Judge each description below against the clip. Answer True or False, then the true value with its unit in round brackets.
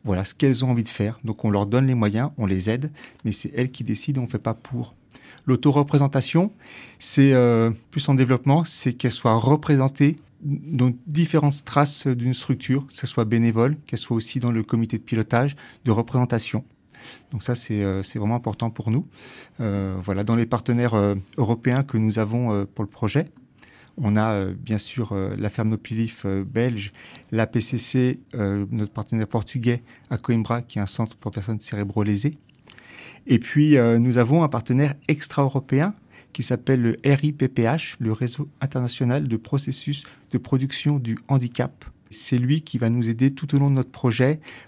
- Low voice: True (125 Hz)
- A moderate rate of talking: True (185 wpm)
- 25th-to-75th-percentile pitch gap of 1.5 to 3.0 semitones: False (3.6 semitones)